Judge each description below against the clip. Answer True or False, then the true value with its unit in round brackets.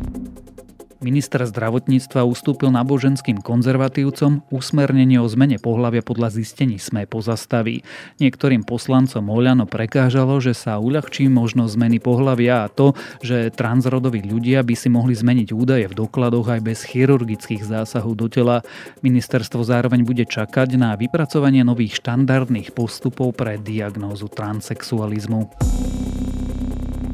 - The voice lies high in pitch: False (120 Hz)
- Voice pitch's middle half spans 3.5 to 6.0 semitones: False (2.6 semitones)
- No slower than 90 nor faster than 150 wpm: True (115 wpm)